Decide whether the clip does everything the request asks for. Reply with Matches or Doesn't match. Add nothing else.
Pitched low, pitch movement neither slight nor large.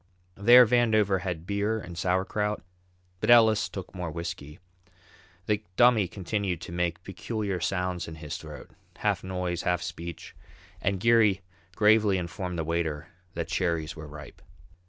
Matches